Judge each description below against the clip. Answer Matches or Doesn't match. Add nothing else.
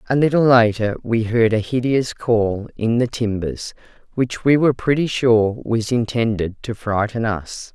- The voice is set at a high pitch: Doesn't match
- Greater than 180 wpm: Doesn't match